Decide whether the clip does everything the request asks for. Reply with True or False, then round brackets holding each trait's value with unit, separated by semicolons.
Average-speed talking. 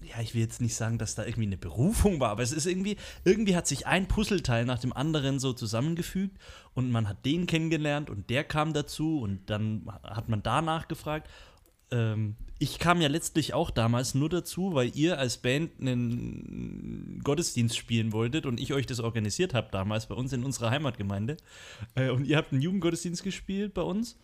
False (195 wpm)